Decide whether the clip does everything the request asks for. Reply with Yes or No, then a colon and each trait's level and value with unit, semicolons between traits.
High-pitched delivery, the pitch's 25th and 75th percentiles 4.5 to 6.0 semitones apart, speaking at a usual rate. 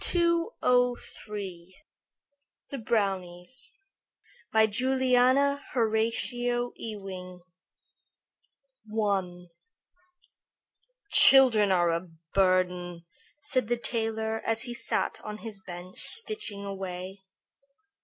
No: high, 220 Hz; average, 5.0 semitones; slow, 75 wpm